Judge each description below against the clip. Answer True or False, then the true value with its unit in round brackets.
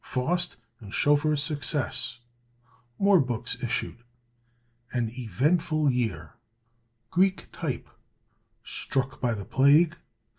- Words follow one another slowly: True (90 wpm)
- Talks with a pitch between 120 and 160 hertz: True (135 Hz)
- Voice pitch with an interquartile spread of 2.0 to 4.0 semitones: False (4.4 semitones)